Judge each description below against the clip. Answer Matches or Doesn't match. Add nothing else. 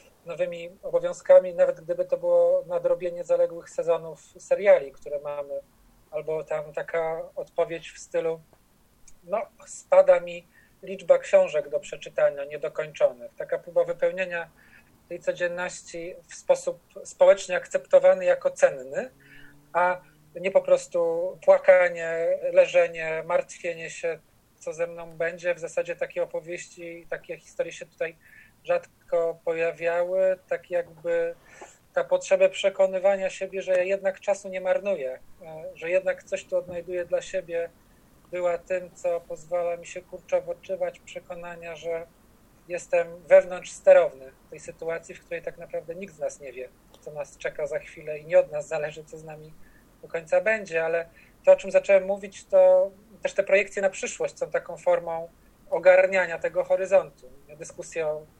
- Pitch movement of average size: Doesn't match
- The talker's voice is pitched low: Doesn't match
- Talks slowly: Doesn't match